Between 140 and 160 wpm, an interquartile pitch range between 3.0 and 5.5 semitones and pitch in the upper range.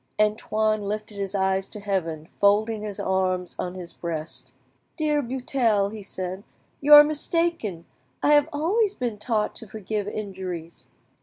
Yes: average, 150 wpm; average, 4.4 semitones; high, 210 Hz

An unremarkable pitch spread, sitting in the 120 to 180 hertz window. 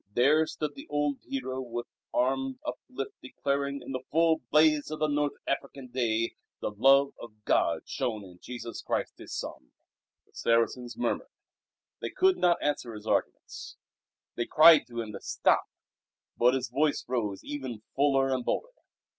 Yes: average, 3.6 semitones; low, 135 Hz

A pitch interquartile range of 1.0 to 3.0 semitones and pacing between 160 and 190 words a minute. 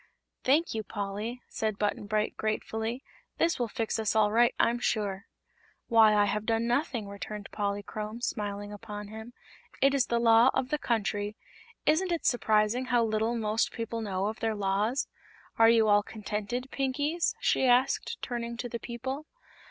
Yes: narrow, 2.5 semitones; average, 165 wpm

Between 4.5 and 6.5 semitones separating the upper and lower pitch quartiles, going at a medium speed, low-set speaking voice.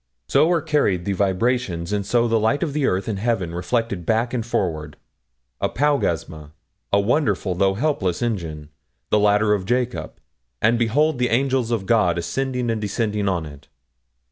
Yes: average, 5.0 semitones; average, 160 wpm; low, 110 Hz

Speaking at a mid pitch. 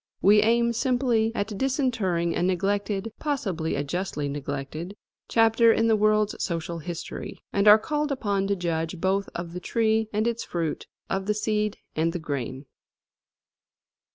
No: high, 200 Hz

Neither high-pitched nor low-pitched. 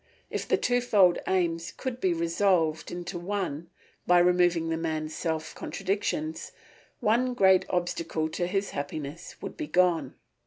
Yes: medium, 175 Hz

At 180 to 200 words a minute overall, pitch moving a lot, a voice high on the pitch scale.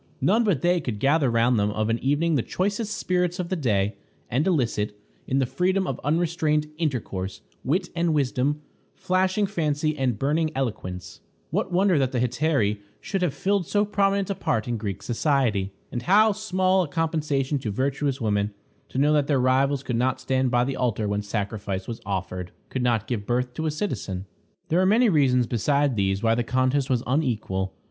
No: average, 190 wpm; wide, 6.7 semitones; low, 135 Hz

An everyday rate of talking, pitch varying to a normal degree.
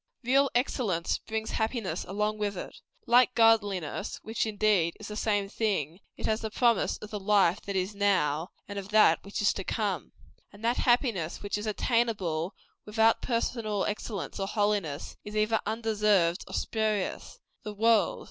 No: average, 165 wpm; narrow, 2.2 semitones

